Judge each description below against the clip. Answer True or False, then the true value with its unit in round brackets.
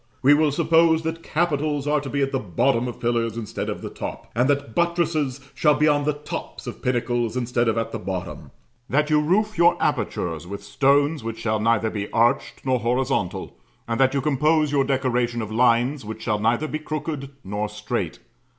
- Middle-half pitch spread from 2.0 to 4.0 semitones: False (4.7 semitones)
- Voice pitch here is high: False (130 Hz)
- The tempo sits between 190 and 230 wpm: True (195 wpm)